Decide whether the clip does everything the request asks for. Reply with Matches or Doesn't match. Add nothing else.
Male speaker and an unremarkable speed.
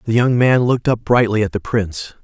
Doesn't match